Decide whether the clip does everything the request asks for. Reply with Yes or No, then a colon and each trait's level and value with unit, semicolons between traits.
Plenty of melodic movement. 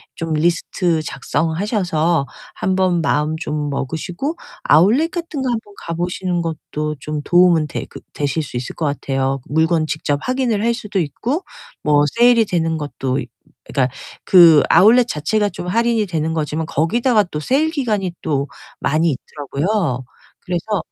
Yes: wide, 5.7 semitones